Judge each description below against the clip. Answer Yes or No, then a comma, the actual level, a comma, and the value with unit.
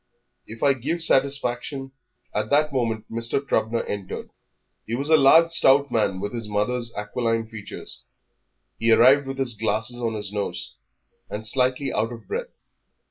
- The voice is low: Yes, low, 120 Hz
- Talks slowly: No, average, 160 wpm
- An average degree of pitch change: Yes, average, 3.6 semitones